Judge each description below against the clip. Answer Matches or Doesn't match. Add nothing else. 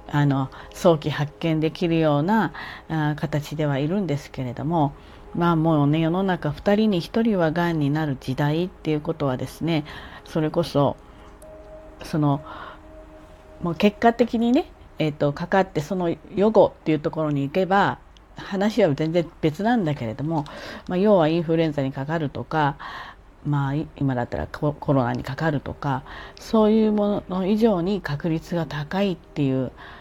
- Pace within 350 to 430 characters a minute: Doesn't match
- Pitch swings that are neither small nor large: Matches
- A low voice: Doesn't match